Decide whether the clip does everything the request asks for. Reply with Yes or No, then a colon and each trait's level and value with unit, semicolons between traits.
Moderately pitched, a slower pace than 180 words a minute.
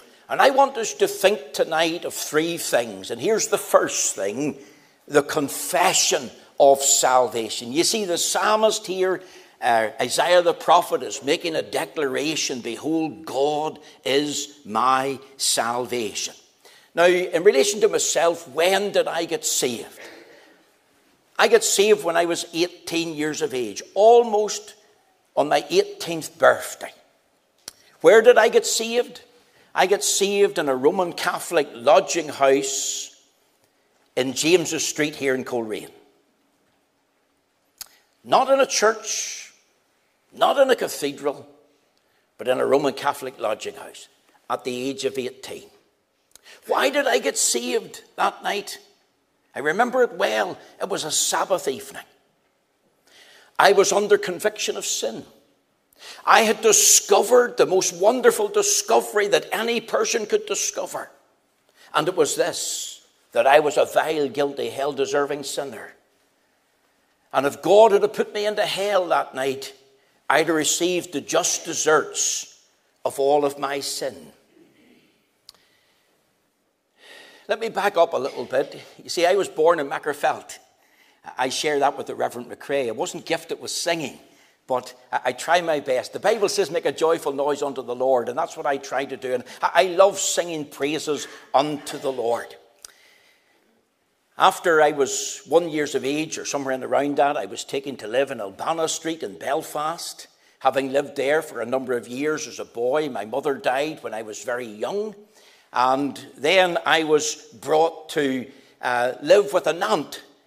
Yes: medium, 170 Hz; average, 150 wpm